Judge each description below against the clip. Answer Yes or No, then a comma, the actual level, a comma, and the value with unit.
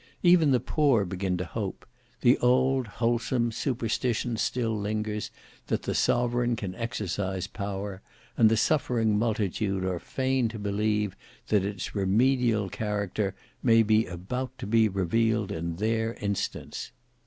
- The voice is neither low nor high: No, low, 110 Hz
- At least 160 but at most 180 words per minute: No, slow, 135 wpm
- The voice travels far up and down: No, average, 3.2 semitones